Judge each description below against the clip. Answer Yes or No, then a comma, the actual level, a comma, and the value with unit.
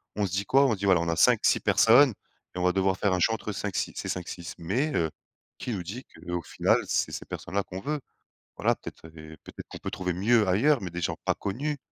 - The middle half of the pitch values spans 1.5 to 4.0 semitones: No, average, 4.5 semitones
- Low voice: Yes, very low, 95 Hz